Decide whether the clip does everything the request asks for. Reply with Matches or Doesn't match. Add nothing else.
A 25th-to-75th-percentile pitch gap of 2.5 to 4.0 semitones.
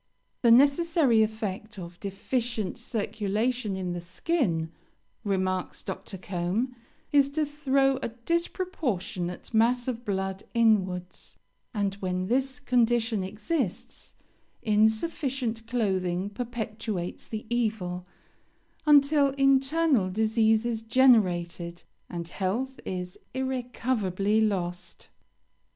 Doesn't match